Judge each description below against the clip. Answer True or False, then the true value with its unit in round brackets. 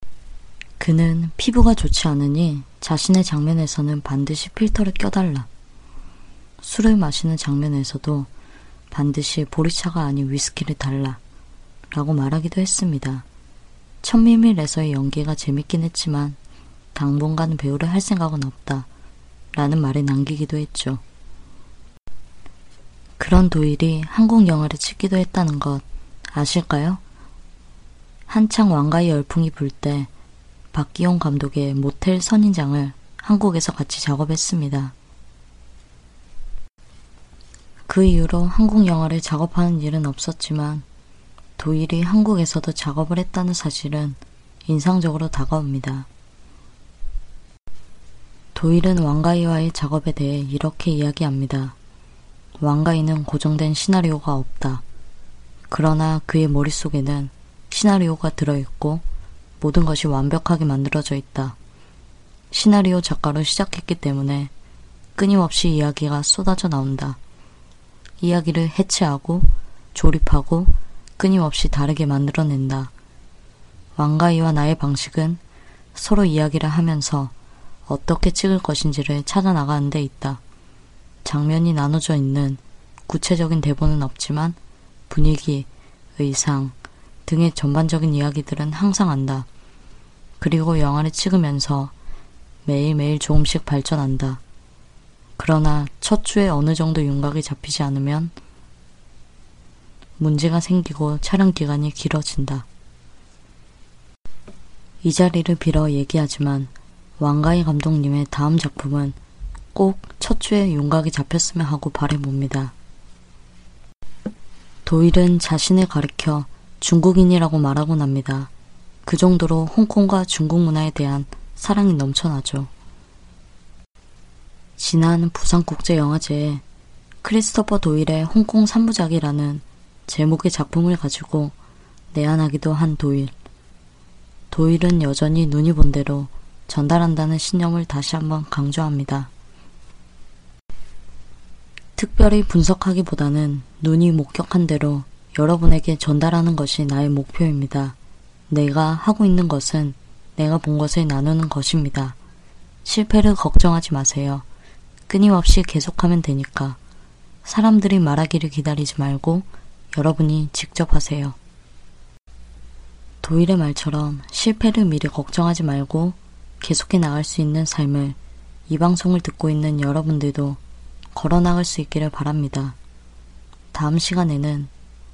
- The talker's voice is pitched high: False (150 Hz)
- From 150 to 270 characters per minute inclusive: True (260 characters per minute)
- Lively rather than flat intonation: False (3.5 semitones)